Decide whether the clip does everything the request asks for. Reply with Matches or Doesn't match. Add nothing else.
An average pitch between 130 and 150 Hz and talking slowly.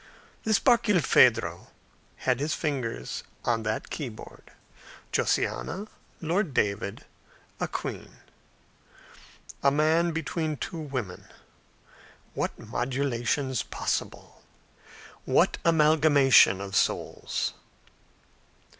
Matches